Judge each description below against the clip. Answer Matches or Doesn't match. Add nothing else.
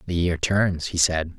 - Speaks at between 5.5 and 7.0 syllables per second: Doesn't match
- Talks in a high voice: Doesn't match